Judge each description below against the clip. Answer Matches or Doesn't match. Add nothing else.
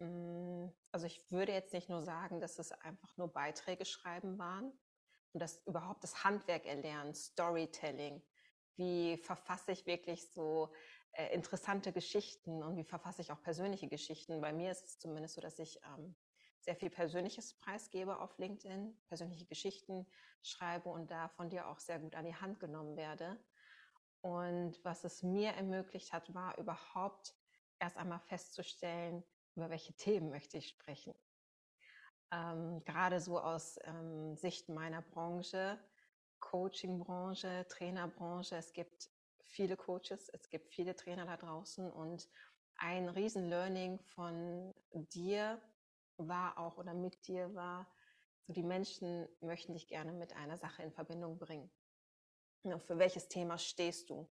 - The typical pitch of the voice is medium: Matches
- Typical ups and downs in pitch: Doesn't match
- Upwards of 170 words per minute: Doesn't match